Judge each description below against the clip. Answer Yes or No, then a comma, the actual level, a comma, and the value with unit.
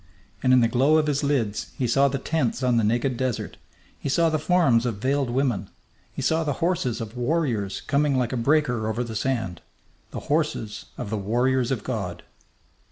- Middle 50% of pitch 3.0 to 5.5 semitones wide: Yes, average, 3.9 semitones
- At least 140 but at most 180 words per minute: No, average, 195 wpm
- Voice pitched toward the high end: No, low, 125 Hz